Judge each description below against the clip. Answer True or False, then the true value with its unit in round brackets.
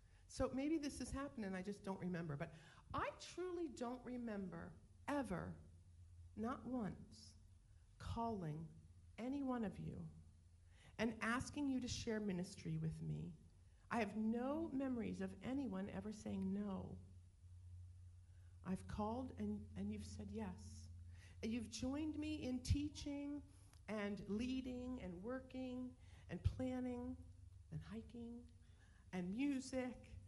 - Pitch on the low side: False (185 Hz)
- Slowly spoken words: True (125 wpm)